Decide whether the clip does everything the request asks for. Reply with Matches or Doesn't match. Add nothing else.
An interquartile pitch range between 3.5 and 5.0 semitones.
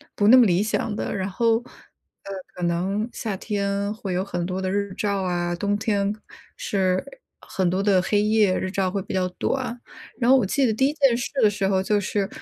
Doesn't match